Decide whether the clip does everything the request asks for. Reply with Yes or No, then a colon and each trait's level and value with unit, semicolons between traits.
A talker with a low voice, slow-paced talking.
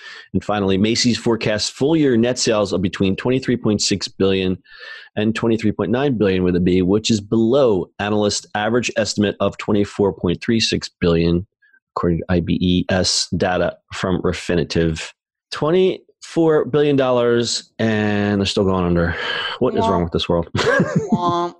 Yes: low, 105 Hz; slow, 130 wpm